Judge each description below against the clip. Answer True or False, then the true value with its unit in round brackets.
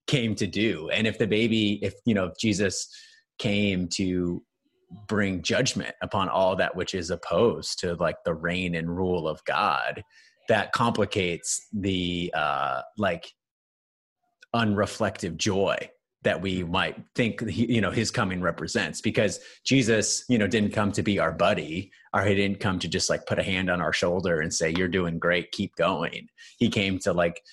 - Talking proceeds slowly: False (175 wpm)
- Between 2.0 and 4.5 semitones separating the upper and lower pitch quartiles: True (4.2 semitones)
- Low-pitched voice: True (100 Hz)